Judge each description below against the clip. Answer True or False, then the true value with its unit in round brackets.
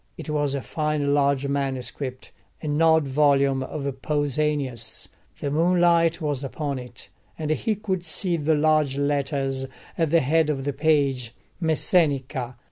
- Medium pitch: True (145 Hz)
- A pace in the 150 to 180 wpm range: False (140 wpm)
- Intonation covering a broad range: False (2.5 semitones)